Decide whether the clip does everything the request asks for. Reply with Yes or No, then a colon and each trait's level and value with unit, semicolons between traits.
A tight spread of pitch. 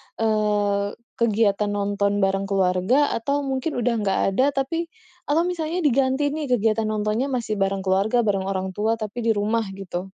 No: average, 4.8 semitones